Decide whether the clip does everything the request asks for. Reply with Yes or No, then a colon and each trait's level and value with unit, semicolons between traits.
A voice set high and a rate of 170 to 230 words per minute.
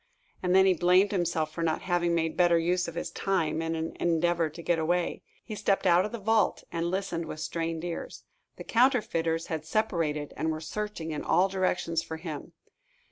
No: medium, 170 Hz; average, 195 wpm